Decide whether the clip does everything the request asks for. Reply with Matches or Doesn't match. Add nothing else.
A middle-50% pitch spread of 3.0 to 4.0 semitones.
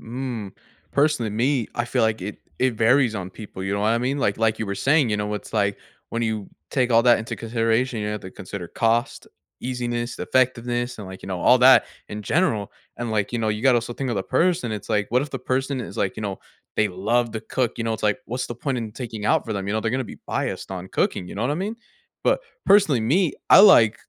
Matches